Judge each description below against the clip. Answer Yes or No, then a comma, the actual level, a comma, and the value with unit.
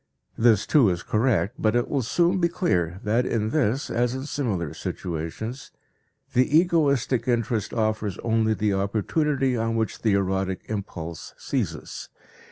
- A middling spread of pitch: Yes, average, 4.6 semitones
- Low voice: Yes, low, 115 Hz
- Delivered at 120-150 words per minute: Yes, average, 145 wpm